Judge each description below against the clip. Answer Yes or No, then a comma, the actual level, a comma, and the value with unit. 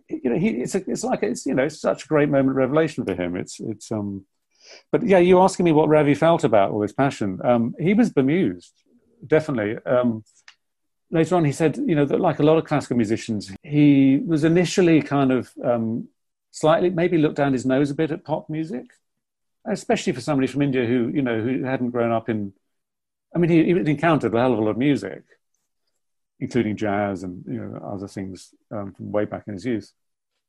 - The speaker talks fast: Yes, fast, 215 wpm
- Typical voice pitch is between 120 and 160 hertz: Yes, low, 135 Hz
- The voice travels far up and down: Yes, wide, 6.1 semitones